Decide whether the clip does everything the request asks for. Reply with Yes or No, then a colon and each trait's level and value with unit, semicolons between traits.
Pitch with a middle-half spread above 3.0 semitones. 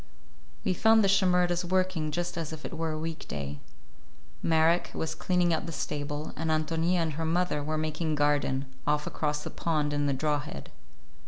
No: average, 2.7 semitones